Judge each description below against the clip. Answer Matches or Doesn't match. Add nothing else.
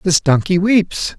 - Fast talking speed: Doesn't match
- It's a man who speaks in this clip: Matches